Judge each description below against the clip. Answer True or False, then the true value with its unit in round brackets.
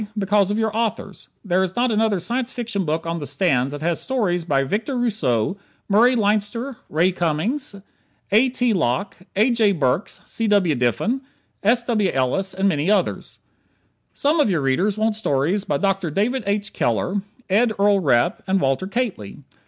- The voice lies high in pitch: True (200 Hz)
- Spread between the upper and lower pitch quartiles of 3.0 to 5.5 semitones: True (5.2 semitones)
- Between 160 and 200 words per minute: True (170 wpm)